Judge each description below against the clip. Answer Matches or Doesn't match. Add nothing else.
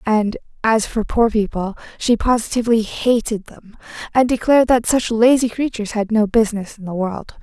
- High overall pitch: Matches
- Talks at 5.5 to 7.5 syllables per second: Doesn't match